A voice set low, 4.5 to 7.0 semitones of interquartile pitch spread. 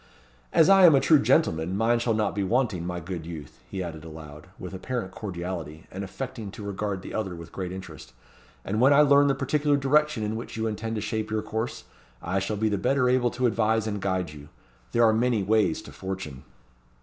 Yes: low, 105 Hz; average, 4.8 semitones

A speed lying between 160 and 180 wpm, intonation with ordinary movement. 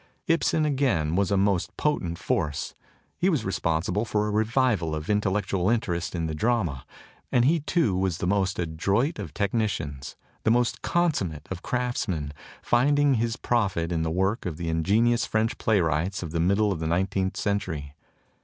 No: average, 165 wpm; wide, 5.9 semitones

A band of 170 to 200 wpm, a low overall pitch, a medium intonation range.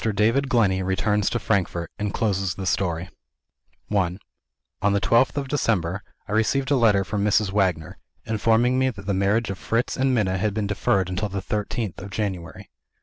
Yes: average, 180 wpm; low, 105 Hz; average, 3.1 semitones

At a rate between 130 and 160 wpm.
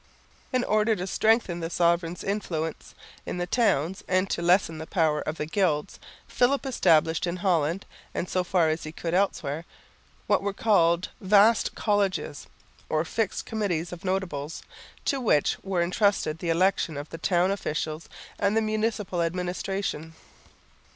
Yes: average, 150 wpm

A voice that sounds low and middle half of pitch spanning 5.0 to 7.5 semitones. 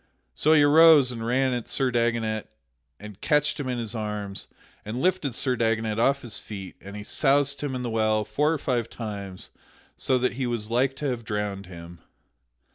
No: low, 120 Hz; average, 4.1 semitones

